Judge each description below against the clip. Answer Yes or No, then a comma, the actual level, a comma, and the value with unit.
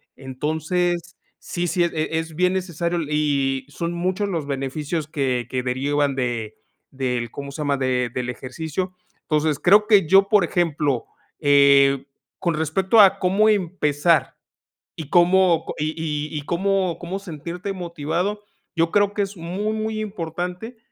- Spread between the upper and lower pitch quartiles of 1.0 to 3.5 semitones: No, average, 4.6 semitones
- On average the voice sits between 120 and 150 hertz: No, medium, 165 Hz